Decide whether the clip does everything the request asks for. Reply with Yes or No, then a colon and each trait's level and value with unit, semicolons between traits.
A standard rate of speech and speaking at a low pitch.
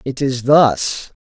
Yes: average, 145 wpm; low, 130 Hz